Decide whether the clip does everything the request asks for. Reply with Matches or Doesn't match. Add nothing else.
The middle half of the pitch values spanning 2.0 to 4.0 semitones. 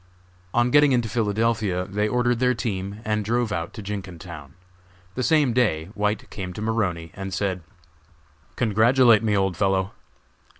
Matches